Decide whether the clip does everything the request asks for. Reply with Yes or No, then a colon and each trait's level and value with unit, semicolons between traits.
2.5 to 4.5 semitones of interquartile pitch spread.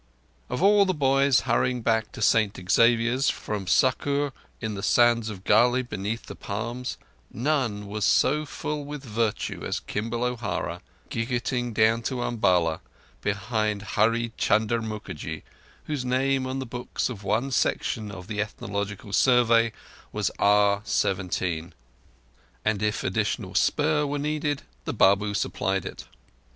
Yes: average, 3.8 semitones